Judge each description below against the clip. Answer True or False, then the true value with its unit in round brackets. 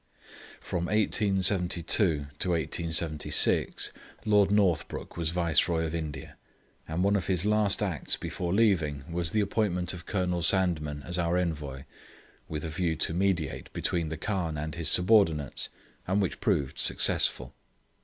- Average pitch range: True (3.3 semitones)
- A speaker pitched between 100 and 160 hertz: False (85 Hz)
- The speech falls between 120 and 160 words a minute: True (140 wpm)